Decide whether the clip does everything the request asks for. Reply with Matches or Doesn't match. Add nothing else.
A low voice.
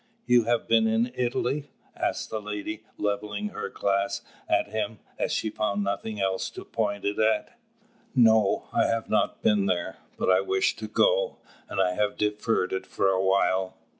Matches